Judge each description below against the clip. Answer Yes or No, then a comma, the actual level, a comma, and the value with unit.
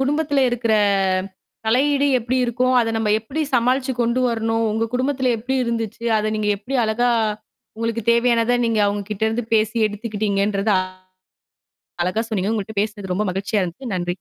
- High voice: Yes, high, 225 Hz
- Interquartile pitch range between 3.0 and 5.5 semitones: No, narrow, 2.6 semitones